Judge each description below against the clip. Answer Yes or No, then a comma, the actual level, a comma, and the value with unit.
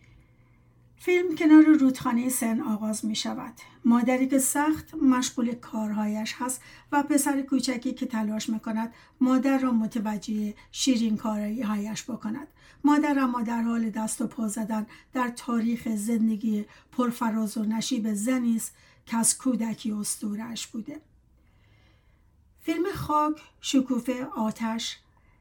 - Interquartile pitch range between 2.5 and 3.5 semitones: Yes, average, 3.0 semitones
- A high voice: Yes, high, 235 Hz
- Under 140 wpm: Yes, average, 120 wpm